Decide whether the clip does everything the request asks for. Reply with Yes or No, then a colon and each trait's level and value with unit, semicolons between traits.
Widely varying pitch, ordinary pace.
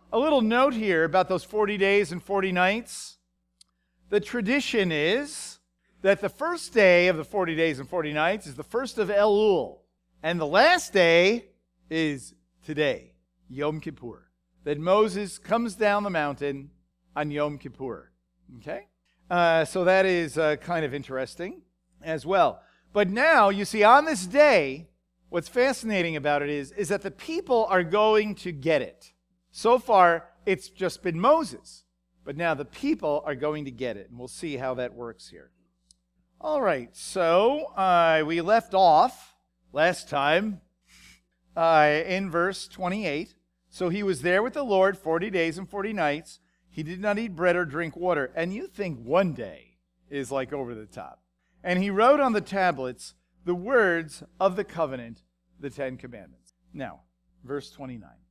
Yes: wide, 7.1 semitones; average, 165 wpm